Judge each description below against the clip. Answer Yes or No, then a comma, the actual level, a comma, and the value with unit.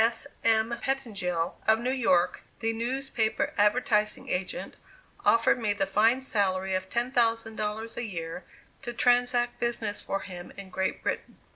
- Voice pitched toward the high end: Yes, high, 225 Hz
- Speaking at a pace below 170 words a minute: Yes, average, 140 wpm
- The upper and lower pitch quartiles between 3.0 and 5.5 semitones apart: Yes, average, 3.7 semitones